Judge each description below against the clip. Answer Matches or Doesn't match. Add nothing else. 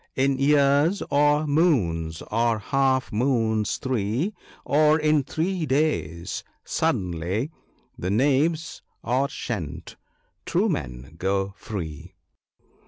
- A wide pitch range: Matches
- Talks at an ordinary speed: Doesn't match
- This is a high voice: Doesn't match